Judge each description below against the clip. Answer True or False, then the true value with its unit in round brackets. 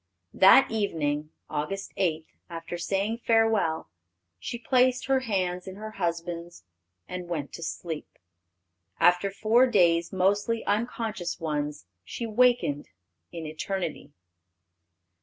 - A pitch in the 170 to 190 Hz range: True (185 Hz)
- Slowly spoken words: True (110 wpm)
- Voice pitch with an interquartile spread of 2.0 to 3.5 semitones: False (5.0 semitones)